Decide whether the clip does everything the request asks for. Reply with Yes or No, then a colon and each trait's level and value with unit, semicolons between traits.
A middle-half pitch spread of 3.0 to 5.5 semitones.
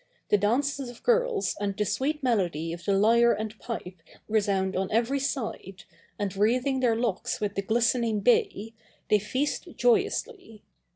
Yes: average, 4.5 semitones